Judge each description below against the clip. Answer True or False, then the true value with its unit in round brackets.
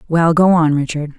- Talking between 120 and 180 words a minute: False (205 wpm)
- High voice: False (160 Hz)